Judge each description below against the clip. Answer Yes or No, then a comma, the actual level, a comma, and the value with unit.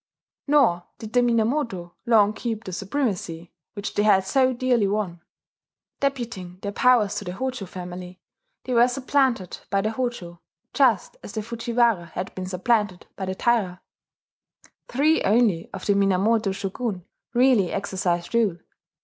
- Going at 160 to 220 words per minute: No, average, 145 wpm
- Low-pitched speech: No, high, 210 Hz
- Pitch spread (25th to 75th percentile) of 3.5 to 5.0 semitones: Yes, average, 4.4 semitones